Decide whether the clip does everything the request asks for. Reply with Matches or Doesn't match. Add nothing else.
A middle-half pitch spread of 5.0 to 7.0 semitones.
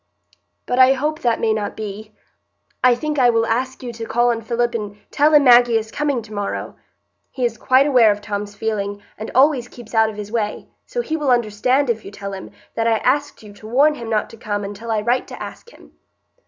Doesn't match